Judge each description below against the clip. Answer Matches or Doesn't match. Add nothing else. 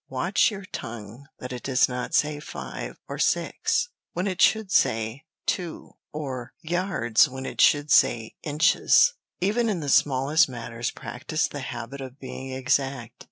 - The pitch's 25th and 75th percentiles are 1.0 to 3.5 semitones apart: Doesn't match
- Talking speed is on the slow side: Doesn't match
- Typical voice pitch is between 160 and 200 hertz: Doesn't match